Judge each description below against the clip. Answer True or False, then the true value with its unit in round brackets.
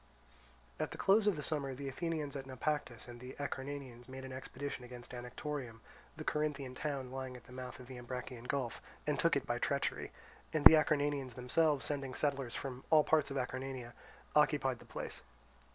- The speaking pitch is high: False (135 Hz)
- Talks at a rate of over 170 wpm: True (185 wpm)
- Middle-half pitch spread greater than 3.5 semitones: False (2.6 semitones)